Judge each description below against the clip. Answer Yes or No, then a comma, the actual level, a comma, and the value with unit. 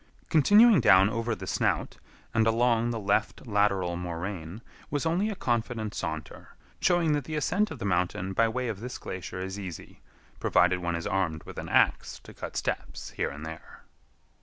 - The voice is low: Yes, low, 105 Hz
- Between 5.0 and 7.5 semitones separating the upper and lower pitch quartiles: Yes, wide, 5.6 semitones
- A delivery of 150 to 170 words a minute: No, average, 180 wpm